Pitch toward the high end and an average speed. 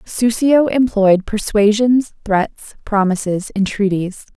No: high, 210 Hz; slow, 80 wpm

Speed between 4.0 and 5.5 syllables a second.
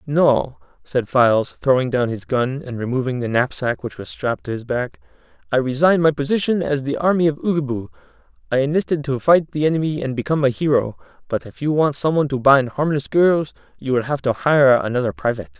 No: 5.8 syllables/s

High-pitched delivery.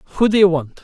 No: medium, 180 Hz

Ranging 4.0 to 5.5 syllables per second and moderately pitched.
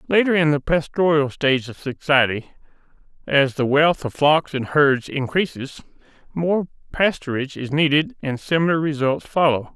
Yes: 4.9 syllables/s; medium, 145 Hz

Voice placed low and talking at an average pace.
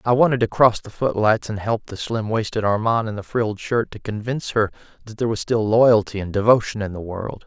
No: low, 110 Hz; fast, 235 wpm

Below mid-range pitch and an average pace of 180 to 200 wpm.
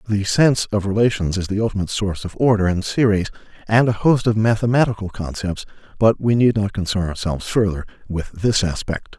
Yes: low, 105 Hz; average, 185 wpm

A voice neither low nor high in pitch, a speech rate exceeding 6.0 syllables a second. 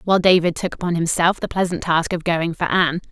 Yes: medium, 170 Hz; 6.2 syllables/s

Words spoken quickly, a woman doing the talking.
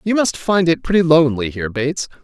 No: fast, 215 wpm; male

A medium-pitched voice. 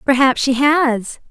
No: very high, 265 Hz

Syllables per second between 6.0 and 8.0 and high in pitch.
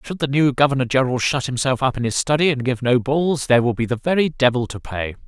No: 6.3 syllables/s; low, 130 Hz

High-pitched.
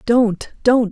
Yes: high, 230 Hz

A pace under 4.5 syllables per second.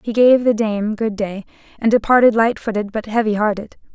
No: 5.1 syllables/s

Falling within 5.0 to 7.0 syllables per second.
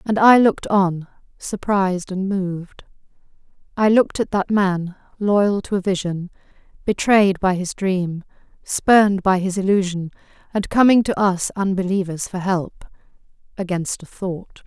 No: 4.5 syllables/s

